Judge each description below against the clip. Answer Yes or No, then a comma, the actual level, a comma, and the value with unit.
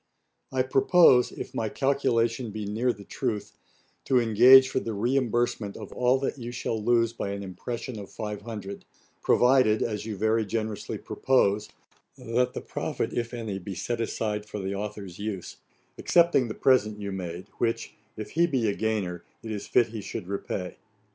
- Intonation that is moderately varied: Yes, average, 3.1 semitones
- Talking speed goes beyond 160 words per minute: Yes, average, 170 wpm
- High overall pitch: No, low, 110 Hz